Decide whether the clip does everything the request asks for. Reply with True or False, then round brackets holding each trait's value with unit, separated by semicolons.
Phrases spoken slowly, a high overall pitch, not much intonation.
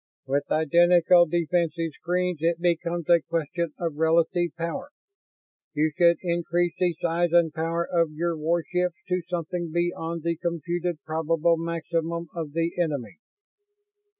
False (130 wpm; 170 Hz; 1.2 semitones)